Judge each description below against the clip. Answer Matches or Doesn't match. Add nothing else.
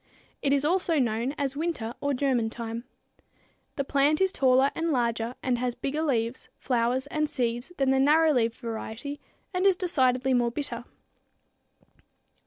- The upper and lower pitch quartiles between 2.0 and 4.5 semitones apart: Matches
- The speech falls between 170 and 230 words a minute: Doesn't match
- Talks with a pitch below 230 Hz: Doesn't match